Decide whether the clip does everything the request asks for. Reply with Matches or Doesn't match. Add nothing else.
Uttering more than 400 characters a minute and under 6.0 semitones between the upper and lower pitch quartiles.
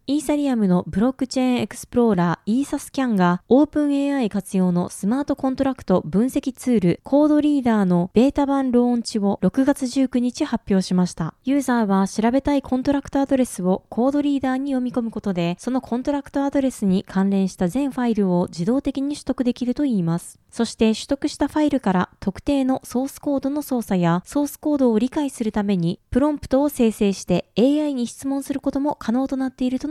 Matches